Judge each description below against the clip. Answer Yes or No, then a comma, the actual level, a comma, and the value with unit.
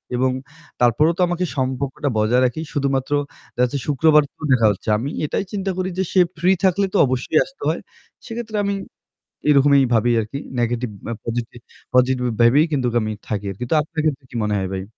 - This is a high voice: No, low, 135 Hz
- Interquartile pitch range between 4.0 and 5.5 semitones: Yes, average, 4.8 semitones